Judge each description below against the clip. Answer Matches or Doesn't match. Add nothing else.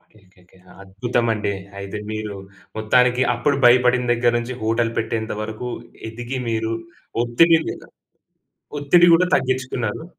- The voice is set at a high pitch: Doesn't match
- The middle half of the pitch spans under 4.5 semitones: Matches